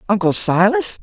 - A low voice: No, high, 205 Hz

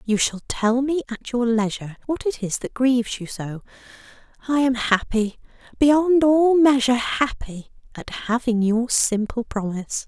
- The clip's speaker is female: Yes, female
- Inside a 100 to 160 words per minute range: Yes, average, 145 wpm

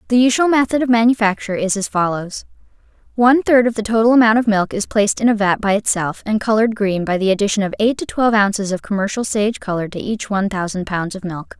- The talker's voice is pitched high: Yes, high, 210 Hz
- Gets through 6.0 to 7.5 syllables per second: Yes, 6.4 syllables/s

